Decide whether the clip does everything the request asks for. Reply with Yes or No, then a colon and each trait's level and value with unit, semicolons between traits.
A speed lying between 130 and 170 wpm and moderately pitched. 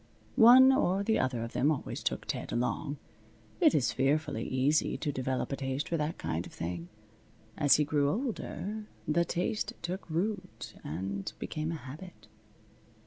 Yes: average, 160 wpm; medium, 150 Hz